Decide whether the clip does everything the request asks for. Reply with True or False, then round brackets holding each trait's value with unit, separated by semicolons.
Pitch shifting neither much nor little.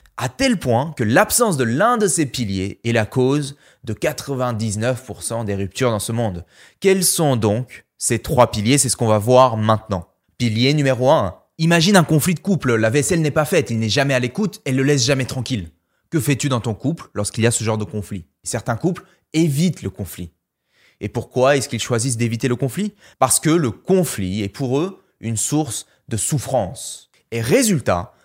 True (5.0 semitones)